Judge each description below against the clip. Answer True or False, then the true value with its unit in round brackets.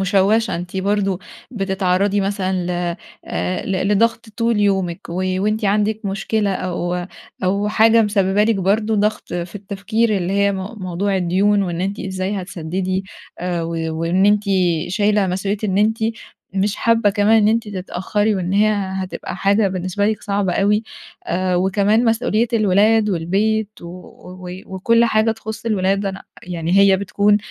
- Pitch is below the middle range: False (200 Hz)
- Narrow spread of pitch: True (2.2 semitones)